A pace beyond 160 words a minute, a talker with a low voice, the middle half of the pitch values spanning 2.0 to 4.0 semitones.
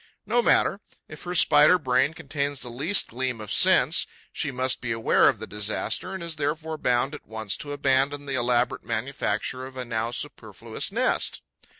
Yes: average, 180 wpm; low, 130 Hz; average, 3.6 semitones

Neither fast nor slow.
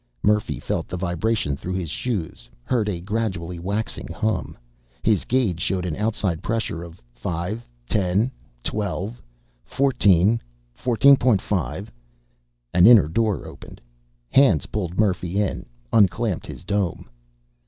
No: slow, 120 wpm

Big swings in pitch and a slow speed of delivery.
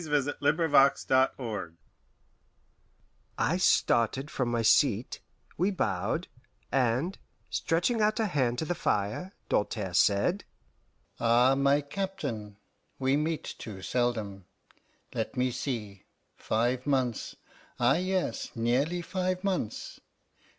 Yes: wide, 6.2 semitones; slow, 115 wpm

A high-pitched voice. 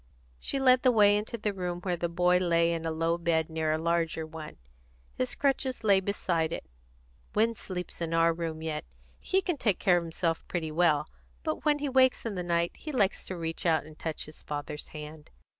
No: medium, 170 Hz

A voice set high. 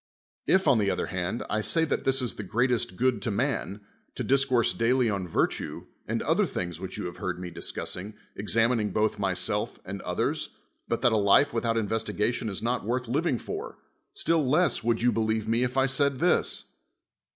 No: low, 115 Hz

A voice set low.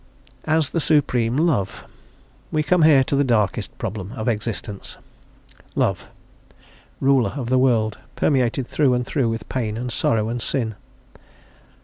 Yes: low, 125 Hz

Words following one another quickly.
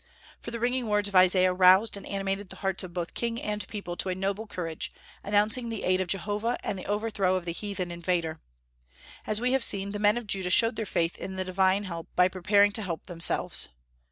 Yes: fast, 220 wpm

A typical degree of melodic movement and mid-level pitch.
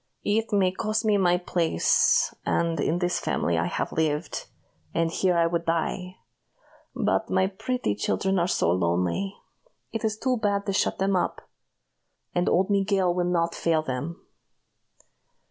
Yes: average, 3.2 semitones; medium, 180 Hz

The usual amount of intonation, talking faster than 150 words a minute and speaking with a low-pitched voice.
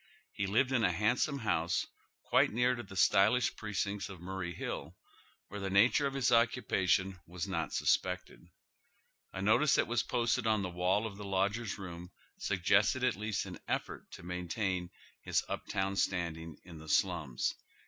Yes: average, 3.8 semitones; average, 170 wpm; low, 100 Hz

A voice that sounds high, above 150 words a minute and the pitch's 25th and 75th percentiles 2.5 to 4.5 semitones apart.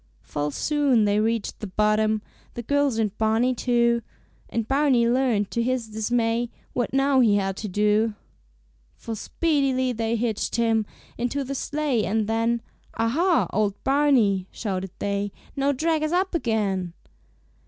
No: high, 230 Hz; average, 145 wpm; average, 3.8 semitones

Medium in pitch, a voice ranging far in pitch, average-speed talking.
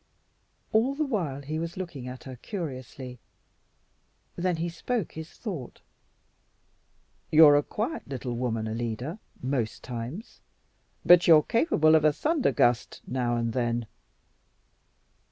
No: medium, 145 Hz; wide, 6.2 semitones; slow, 125 wpm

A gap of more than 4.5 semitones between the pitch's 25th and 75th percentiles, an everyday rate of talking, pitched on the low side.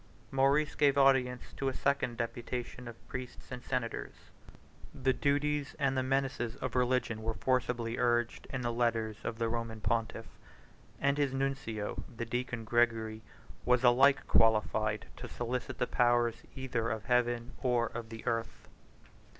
No: narrow, 2.4 semitones; average, 150 wpm; low, 120 Hz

